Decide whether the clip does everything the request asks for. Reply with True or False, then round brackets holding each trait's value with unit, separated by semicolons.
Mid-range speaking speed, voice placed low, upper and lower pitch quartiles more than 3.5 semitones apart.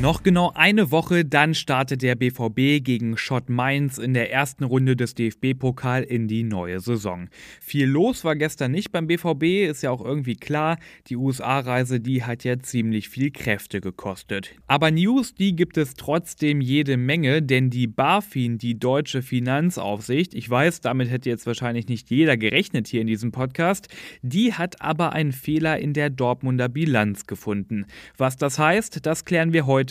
True (175 wpm; 130 Hz; 4.5 semitones)